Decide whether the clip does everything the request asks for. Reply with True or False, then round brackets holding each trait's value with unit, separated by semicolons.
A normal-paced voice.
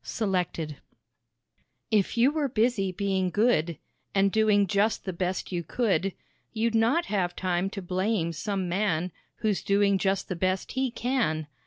True (150 wpm)